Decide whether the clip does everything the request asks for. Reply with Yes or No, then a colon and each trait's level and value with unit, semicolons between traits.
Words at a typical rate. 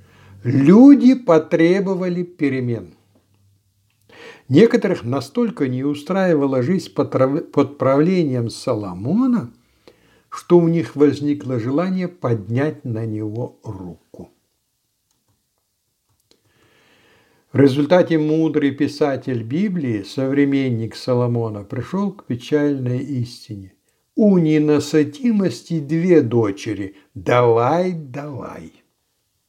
No: slow, 75 wpm